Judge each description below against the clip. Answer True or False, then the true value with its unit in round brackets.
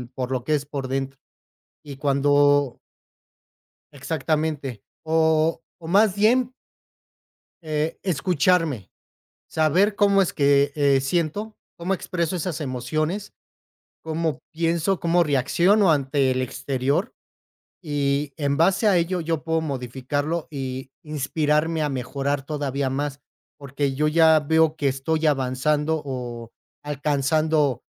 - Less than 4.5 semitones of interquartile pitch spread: True (3.0 semitones)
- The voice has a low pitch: False (150 Hz)